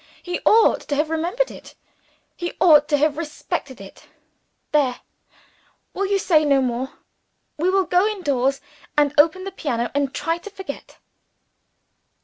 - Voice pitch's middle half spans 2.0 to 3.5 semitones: No, average, 4.8 semitones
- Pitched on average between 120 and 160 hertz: No, very high, 310 Hz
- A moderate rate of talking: Yes, average, 145 wpm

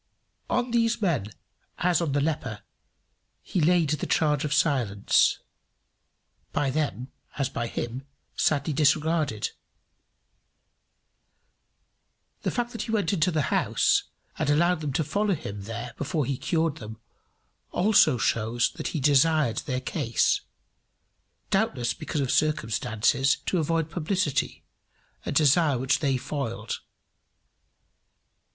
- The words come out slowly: Yes, slow, 125 wpm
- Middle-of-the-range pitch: Yes, medium, 150 Hz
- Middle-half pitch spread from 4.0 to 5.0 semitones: Yes, average, 4.4 semitones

